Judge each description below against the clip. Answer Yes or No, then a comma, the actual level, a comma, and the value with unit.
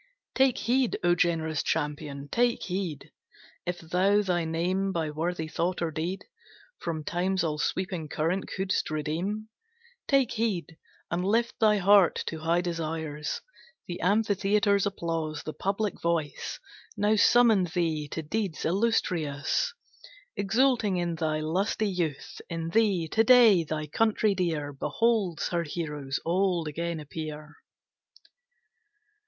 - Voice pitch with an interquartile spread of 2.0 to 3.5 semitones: No, average, 4.2 semitones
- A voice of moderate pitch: Yes, medium, 175 Hz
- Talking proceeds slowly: Yes, slow, 125 wpm